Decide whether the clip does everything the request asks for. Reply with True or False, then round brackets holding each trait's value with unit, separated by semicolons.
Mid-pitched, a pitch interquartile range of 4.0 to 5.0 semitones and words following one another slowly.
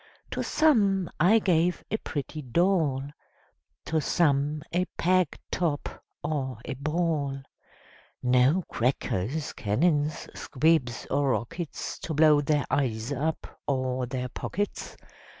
True (150 Hz; 4.4 semitones; 115 wpm)